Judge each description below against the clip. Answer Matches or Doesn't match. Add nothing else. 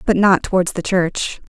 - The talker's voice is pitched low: Doesn't match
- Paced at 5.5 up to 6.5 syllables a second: Doesn't match